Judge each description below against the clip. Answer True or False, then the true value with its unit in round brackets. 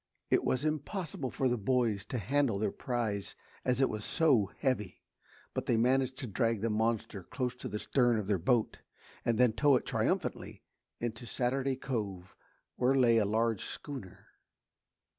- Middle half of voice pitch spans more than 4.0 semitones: False (3.5 semitones)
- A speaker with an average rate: True (170 wpm)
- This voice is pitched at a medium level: False (120 Hz)